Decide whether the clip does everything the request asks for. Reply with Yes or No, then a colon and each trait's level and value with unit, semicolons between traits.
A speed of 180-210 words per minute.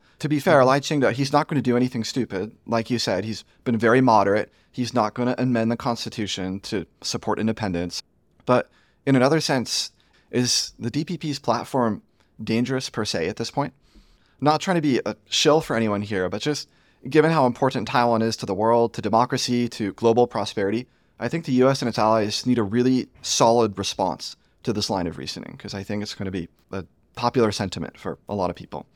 Yes: fast, 205 wpm